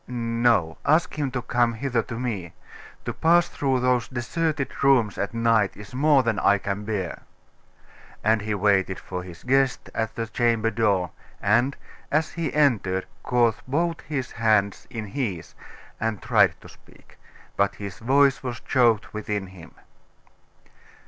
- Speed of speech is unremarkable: Yes, average, 150 wpm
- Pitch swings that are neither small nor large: Yes, average, 4.3 semitones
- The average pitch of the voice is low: Yes, low, 115 Hz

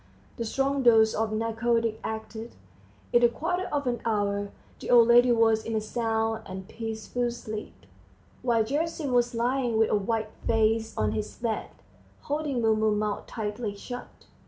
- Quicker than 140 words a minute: Yes, average, 160 wpm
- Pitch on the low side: No, high, 225 Hz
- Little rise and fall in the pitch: Yes, narrow, 1.8 semitones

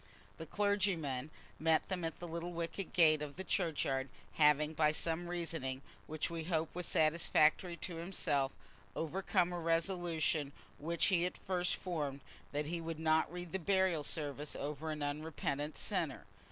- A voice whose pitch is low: No, medium, 160 Hz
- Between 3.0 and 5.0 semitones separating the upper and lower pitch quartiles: No, narrow, 2.6 semitones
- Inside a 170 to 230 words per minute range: No, average, 155 wpm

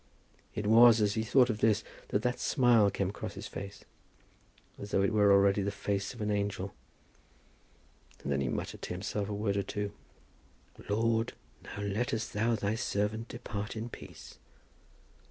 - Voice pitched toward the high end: No, low, 105 Hz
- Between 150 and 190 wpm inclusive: Yes, average, 170 wpm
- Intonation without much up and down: Yes, narrow, 1.9 semitones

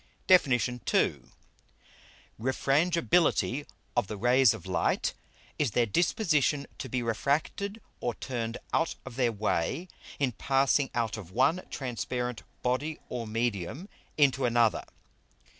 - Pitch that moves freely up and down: No, average, 3.8 semitones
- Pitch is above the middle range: No, low, 125 Hz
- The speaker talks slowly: Yes, slow, 120 wpm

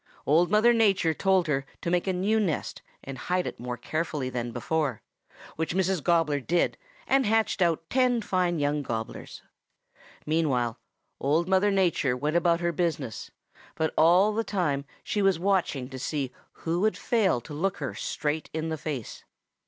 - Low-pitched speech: No, medium, 165 Hz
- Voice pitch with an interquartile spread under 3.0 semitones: No, average, 4.8 semitones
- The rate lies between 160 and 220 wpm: Yes, average, 170 wpm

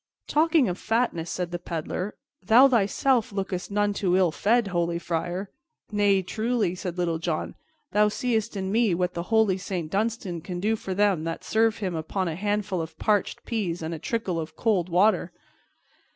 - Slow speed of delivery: No, average, 180 wpm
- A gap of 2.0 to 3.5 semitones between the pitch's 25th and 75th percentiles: No, average, 3.9 semitones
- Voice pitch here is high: Yes, high, 195 Hz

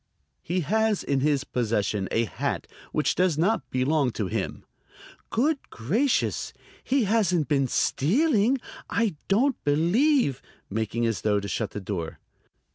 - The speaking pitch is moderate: Yes, medium, 150 Hz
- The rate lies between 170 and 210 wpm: No, slow, 135 wpm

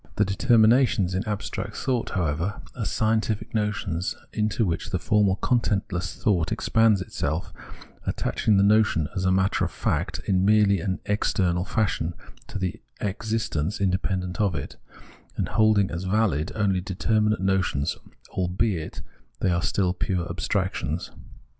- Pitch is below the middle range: Yes, very low, 95 Hz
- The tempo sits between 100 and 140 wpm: Yes, slow, 135 wpm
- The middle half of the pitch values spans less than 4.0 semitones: Yes, average, 3.0 semitones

